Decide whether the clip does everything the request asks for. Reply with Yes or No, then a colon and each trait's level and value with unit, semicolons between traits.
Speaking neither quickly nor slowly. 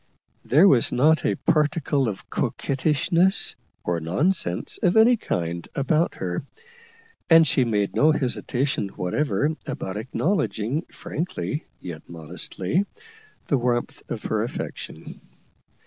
No: slow, 115 wpm